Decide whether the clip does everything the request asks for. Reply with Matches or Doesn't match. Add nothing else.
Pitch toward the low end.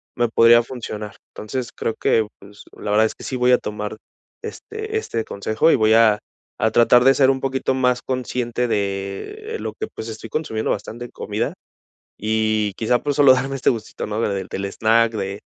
Matches